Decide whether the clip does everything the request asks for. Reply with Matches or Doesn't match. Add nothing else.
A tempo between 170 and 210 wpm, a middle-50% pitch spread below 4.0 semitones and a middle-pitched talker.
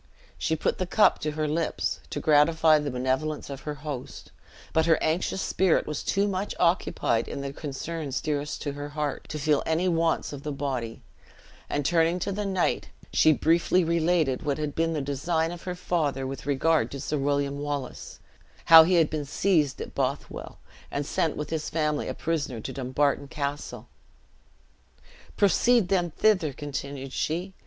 Matches